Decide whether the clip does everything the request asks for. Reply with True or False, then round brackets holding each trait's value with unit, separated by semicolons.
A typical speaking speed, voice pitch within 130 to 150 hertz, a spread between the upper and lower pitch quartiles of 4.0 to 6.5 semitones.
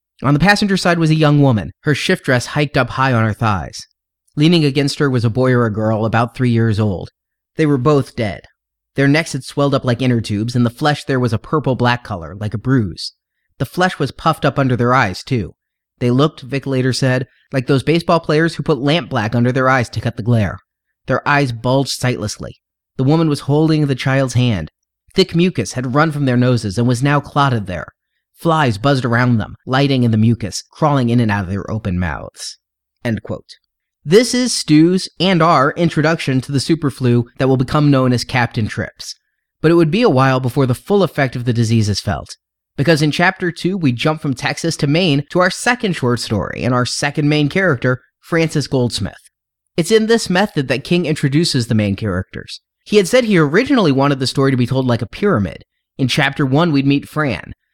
False (215 wpm; 135 Hz; 4.4 semitones)